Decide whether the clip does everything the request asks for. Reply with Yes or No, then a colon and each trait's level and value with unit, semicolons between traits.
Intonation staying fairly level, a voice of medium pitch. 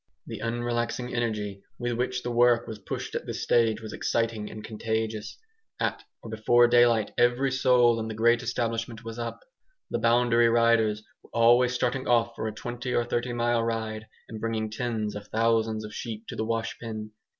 No: narrow, 1.4 semitones; low, 115 Hz